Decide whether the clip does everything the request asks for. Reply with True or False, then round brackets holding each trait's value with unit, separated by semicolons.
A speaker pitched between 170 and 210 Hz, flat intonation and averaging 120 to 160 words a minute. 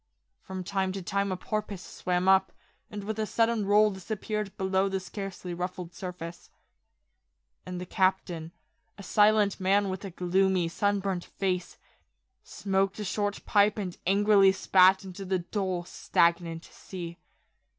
True (190 Hz; 1.9 semitones; 140 wpm)